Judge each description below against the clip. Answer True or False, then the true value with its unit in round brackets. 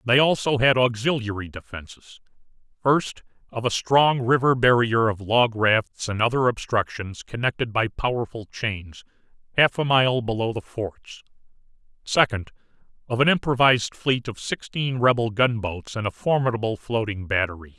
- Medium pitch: False (115 Hz)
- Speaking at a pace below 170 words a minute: True (140 wpm)